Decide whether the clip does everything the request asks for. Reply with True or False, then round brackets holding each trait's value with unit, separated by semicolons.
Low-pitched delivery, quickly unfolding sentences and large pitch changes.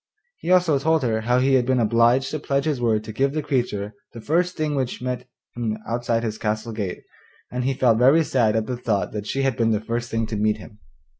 False (120 Hz; 240 wpm; 3.5 semitones)